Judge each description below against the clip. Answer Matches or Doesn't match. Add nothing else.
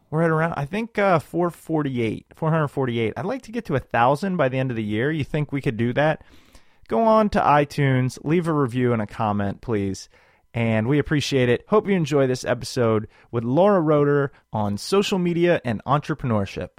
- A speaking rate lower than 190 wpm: Doesn't match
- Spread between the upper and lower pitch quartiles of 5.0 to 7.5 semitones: Matches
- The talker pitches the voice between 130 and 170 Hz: Matches